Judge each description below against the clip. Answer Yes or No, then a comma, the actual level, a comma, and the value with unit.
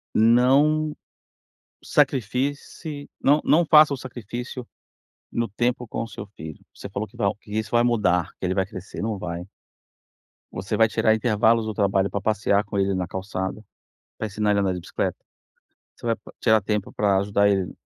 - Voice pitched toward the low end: Yes, low, 105 Hz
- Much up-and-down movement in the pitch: No, average, 3.6 semitones